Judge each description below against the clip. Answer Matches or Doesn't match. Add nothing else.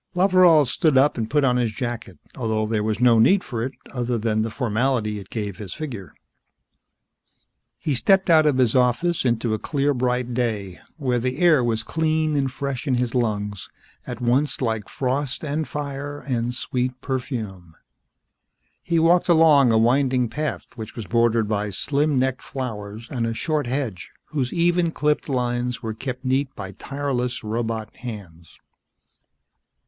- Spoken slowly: Doesn't match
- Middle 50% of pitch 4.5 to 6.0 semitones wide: Doesn't match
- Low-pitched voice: Matches